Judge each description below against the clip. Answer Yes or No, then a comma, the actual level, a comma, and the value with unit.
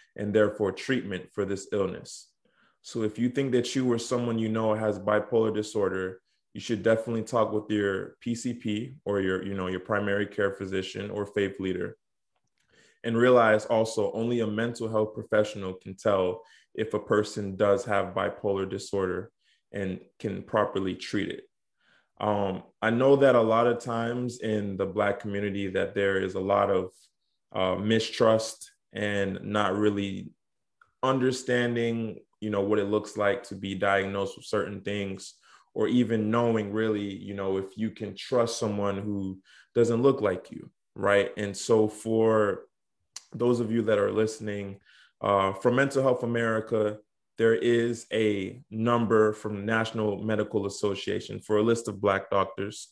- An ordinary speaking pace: Yes, average, 160 wpm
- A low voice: Yes, low, 105 Hz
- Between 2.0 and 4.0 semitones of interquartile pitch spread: Yes, narrow, 2.5 semitones